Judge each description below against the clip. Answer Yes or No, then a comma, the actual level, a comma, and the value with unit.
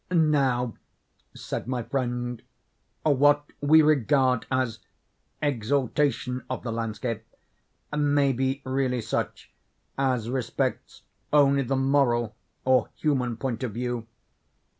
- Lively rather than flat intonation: No, narrow, 2.5 semitones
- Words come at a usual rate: No, slow, 105 wpm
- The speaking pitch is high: No, low, 130 Hz